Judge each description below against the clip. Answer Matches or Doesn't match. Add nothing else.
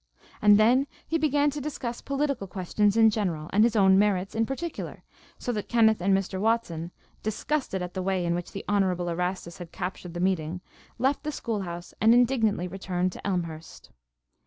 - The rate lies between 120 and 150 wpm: Doesn't match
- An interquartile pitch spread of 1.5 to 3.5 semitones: Doesn't match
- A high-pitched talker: Matches